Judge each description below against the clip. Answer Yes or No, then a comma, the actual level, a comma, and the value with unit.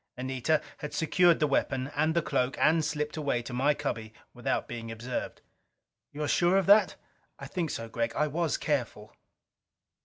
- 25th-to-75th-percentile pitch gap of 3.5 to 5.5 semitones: Yes, average, 4.3 semitones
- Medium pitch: Yes, medium, 145 Hz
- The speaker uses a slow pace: No, average, 165 wpm